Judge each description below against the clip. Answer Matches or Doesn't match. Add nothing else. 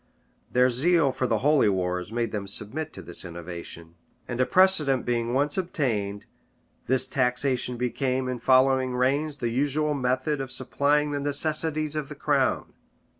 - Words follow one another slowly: Doesn't match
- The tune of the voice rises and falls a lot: Doesn't match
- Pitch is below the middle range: Matches